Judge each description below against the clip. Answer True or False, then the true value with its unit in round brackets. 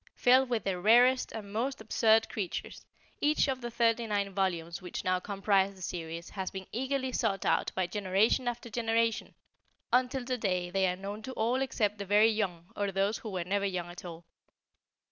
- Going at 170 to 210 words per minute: True (185 wpm)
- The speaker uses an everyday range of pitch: True (3.9 semitones)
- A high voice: True (205 Hz)